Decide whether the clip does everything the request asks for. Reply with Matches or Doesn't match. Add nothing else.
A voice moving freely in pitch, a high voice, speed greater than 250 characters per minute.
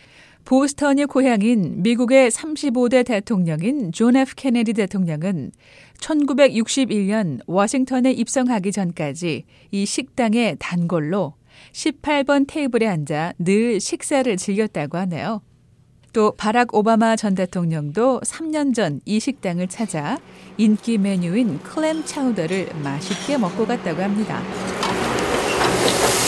Doesn't match